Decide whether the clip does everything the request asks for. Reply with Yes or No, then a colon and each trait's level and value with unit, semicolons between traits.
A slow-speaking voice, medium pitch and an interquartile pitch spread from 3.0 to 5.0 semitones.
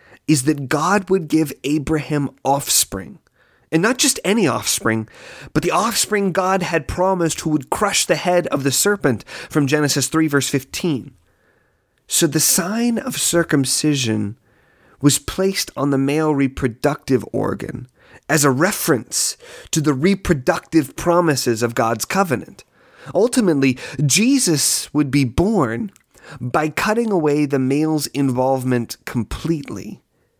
Yes: slow, 130 wpm; medium, 150 Hz; average, 4.3 semitones